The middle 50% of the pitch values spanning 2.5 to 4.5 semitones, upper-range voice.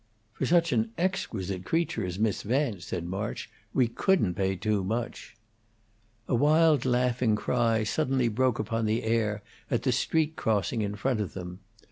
No: average, 4.1 semitones; low, 115 Hz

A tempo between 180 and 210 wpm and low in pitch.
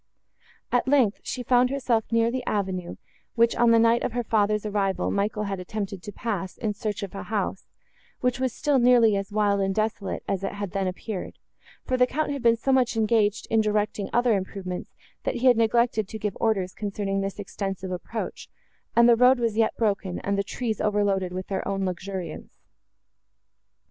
No: average, 190 wpm; high, 210 Hz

